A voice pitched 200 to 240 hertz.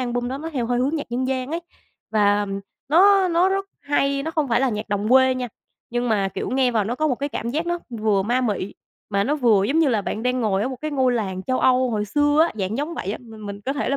No: very high, 250 Hz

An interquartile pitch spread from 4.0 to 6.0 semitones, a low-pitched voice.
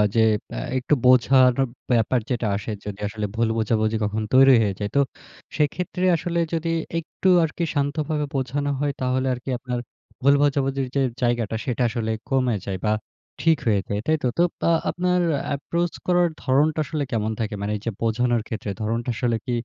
Yes: average, 4.6 semitones; low, 125 Hz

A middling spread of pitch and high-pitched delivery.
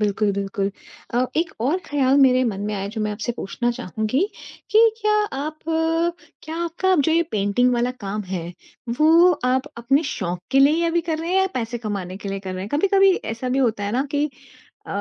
No: wide, 7.6 semitones; very high, 250 Hz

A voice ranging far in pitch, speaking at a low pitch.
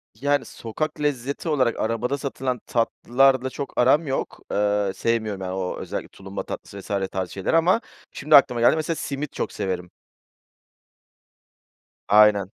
Yes: wide, 5.7 semitones; low, 120 Hz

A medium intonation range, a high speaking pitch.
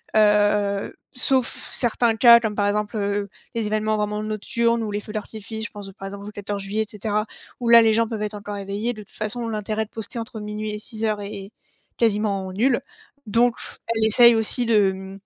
No: narrow, 1.7 semitones; high, 215 Hz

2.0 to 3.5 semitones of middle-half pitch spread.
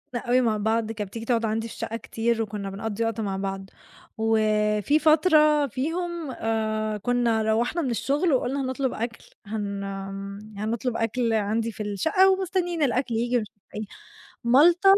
No: average, 4.0 semitones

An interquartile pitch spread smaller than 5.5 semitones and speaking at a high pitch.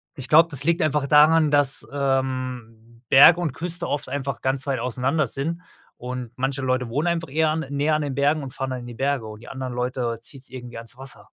No: average, 2.8 semitones; low, 135 Hz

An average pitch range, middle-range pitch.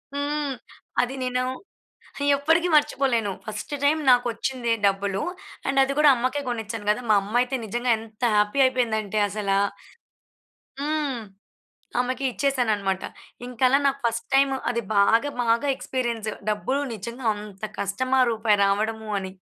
No: average, 3.9 semitones; high, 235 Hz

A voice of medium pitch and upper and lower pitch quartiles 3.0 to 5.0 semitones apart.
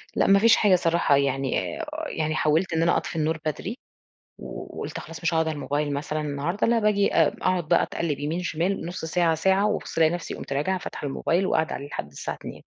Yes: medium, 165 Hz; average, 3.5 semitones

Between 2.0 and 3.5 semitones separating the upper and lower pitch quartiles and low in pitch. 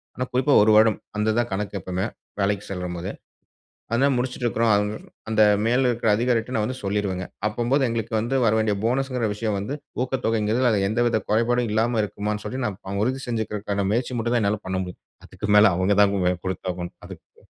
Yes: average, 3.0 semitones; low, 110 Hz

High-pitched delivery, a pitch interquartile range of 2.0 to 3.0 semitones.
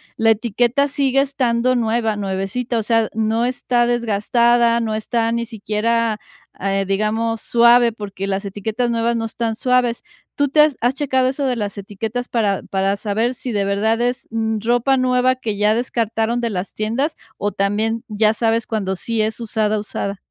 Yes: high, 225 Hz; narrow, 2.4 semitones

